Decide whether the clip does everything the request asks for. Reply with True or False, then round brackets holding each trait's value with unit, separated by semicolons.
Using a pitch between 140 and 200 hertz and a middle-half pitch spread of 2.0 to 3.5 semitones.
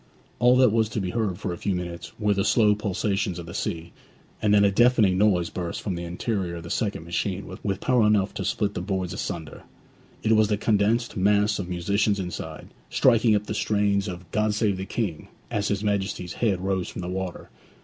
False (100 Hz; 2.7 semitones)